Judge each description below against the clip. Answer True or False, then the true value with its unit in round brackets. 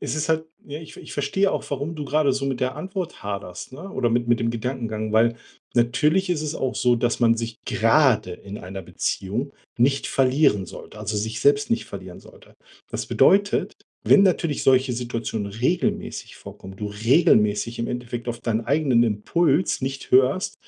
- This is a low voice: True (125 Hz)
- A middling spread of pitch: True (4.7 semitones)